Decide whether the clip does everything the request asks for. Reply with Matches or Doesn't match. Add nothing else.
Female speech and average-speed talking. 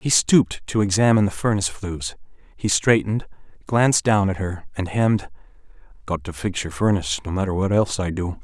Doesn't match